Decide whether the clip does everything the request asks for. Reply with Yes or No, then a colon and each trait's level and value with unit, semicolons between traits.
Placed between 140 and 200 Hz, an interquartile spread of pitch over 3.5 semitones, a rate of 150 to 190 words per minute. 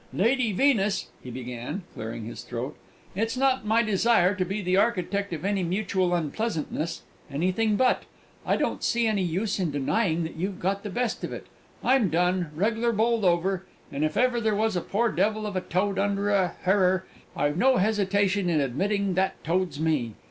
Yes: high, 190 Hz; average, 4.0 semitones; average, 185 wpm